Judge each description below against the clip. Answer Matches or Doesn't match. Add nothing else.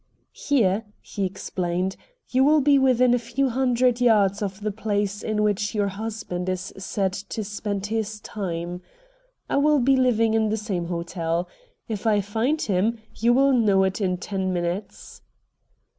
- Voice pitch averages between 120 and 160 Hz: Doesn't match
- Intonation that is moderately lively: Matches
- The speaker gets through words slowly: Doesn't match